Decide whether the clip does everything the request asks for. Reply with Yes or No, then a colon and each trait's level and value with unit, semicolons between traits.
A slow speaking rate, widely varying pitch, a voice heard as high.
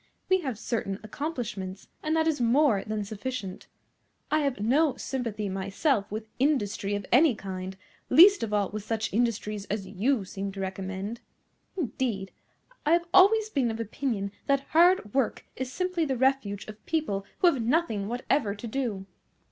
No: average, 165 wpm; wide, 5.9 semitones; high, 230 Hz